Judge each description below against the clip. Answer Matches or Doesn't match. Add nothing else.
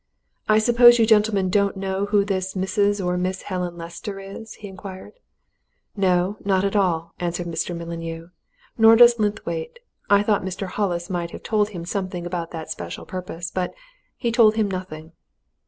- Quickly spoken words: Doesn't match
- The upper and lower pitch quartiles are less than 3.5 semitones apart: Matches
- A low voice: Doesn't match